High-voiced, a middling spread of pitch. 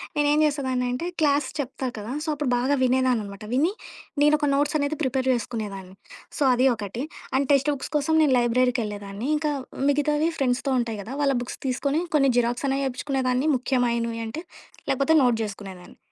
Yes: very high, 260 Hz; average, 3.3 semitones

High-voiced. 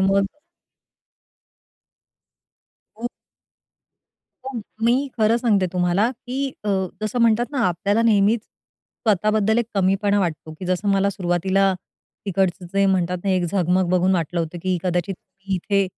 Yes: high, 195 Hz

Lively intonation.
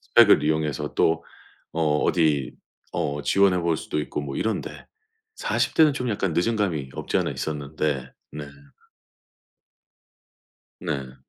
No: average, 3.5 semitones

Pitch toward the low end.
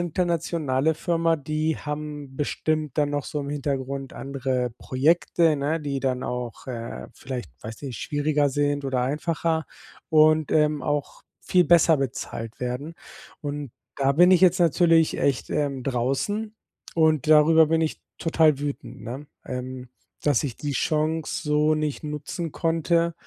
No: medium, 150 Hz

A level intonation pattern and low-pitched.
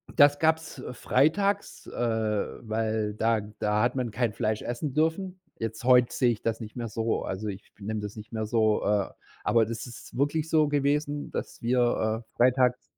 No: average, 4.5 semitones; low, 120 Hz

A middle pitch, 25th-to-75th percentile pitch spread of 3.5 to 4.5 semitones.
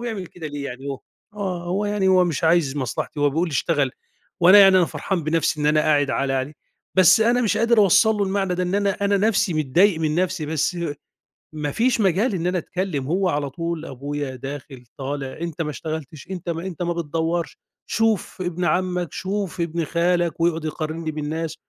Yes: medium, 170 Hz; average, 3.9 semitones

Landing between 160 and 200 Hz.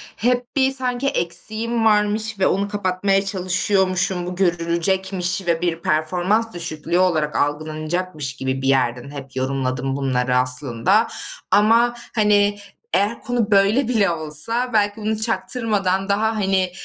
Yes: high, 190 Hz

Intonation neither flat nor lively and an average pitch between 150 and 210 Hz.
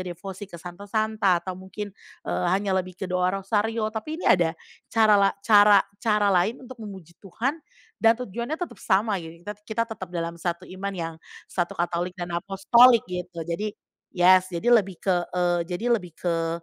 Yes: average, 3.4 semitones; high, 190 Hz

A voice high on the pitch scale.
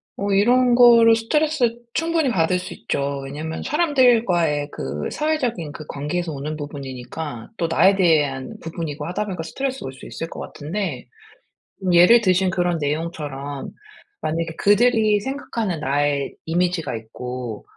No: medium, 170 Hz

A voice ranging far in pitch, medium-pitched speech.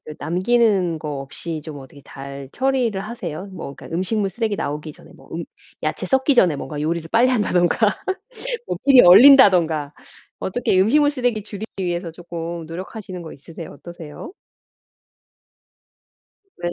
Yes: wide, 5.7 semitones; medium, 180 Hz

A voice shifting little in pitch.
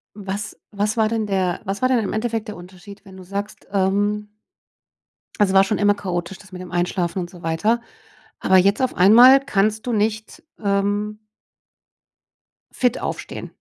Yes: narrow, 2.2 semitones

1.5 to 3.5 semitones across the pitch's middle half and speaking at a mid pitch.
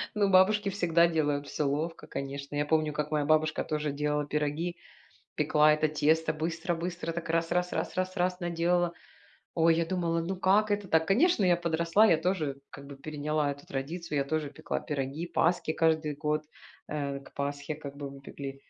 Yes: average, 2.9 semitones; medium, 160 Hz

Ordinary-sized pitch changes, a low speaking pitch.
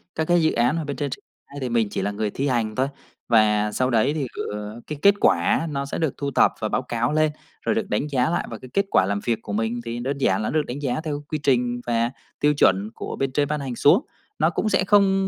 Yes: average, 4.7 semitones; low, 130 Hz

